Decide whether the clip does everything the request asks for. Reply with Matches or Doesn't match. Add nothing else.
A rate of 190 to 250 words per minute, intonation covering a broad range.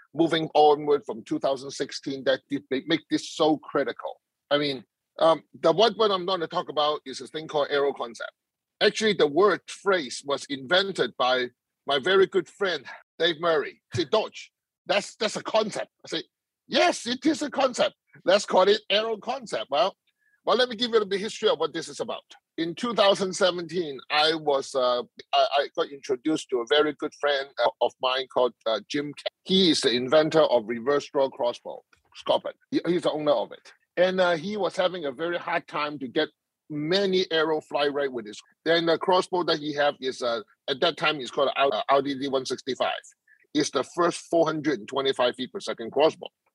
Matches